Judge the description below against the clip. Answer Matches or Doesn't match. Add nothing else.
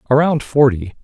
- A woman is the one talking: Doesn't match